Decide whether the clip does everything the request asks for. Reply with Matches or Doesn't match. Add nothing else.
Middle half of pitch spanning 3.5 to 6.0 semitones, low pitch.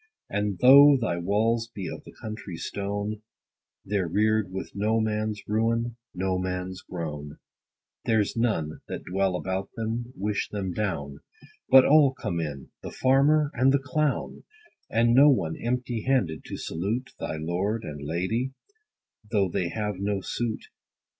Matches